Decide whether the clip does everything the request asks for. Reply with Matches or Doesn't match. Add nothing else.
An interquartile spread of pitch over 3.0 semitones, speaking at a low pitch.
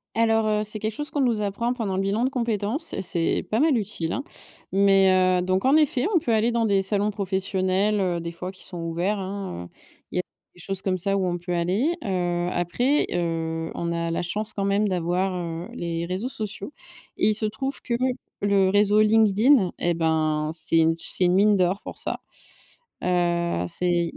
Doesn't match